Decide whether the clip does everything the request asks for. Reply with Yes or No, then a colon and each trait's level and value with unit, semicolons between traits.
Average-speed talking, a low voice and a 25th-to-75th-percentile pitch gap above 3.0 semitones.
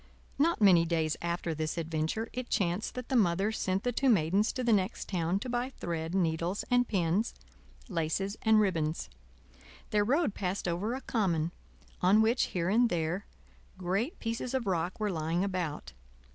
No: average, 170 wpm; high, 190 Hz; average, 5.0 semitones